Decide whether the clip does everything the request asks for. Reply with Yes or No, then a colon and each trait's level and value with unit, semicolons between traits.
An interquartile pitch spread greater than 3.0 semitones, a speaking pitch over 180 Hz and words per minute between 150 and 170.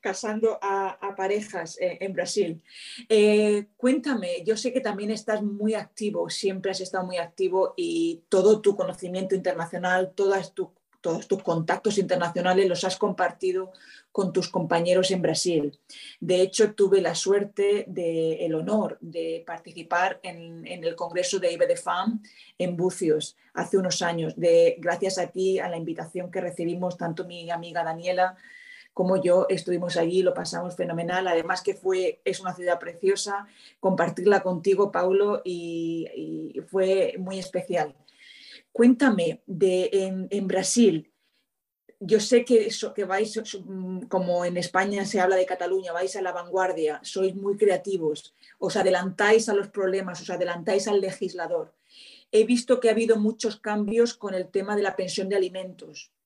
No: average, 2.7 semitones; high, 190 Hz; average, 155 wpm